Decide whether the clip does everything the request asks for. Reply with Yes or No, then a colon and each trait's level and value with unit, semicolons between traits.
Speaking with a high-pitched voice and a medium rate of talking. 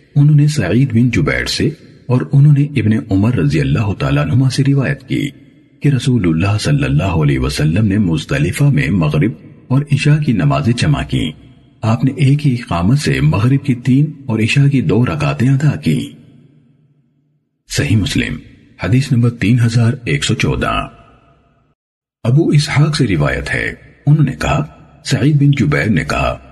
No: low, 135 Hz; average, 165 wpm